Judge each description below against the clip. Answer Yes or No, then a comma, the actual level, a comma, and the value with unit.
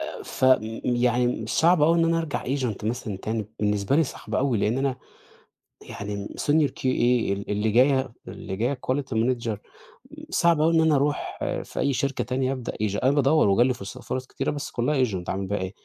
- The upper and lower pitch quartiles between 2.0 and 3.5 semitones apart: No, average, 4.5 semitones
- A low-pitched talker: Yes, low, 125 Hz